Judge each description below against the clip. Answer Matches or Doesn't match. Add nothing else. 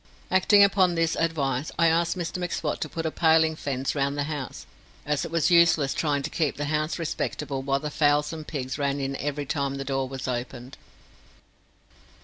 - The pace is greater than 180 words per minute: Matches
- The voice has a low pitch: Doesn't match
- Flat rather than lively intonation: Doesn't match